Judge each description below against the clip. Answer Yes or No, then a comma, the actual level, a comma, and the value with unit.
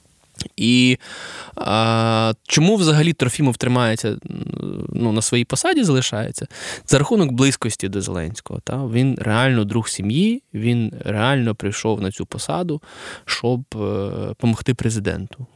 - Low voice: Yes, low, 120 Hz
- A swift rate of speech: No, average, 120 wpm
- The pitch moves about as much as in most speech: Yes, average, 3.9 semitones